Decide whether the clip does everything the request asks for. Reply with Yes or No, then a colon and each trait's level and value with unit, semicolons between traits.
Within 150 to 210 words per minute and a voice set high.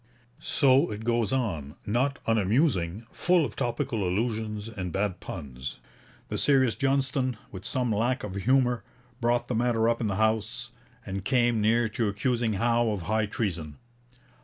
No: average, 155 wpm; low, 115 Hz